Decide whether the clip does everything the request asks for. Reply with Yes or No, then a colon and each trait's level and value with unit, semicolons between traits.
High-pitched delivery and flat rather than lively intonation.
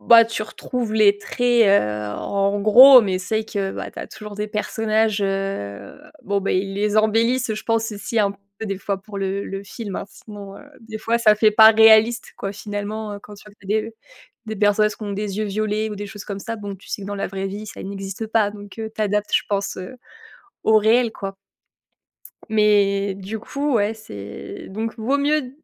Yes: high, 210 Hz; narrow, 1.8 semitones